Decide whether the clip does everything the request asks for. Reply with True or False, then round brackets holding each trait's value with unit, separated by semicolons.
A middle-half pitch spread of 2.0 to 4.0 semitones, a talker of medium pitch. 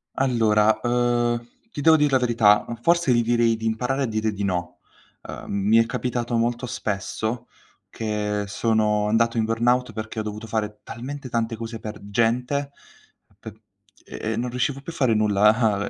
False (2.4 semitones; 115 Hz)